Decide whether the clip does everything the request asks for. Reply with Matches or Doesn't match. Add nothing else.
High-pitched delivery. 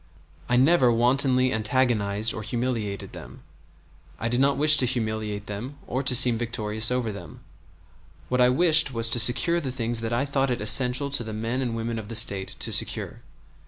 Doesn't match